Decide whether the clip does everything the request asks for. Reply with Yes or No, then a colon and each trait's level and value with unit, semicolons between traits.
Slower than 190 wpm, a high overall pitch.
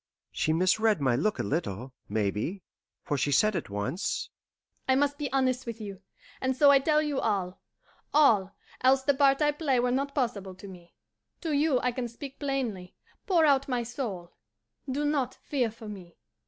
Yes: average, 180 wpm; high, 240 Hz